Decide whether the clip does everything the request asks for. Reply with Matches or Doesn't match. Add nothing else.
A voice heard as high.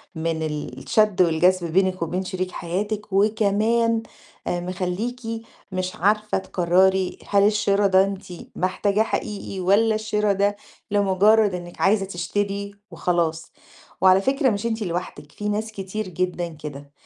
Matches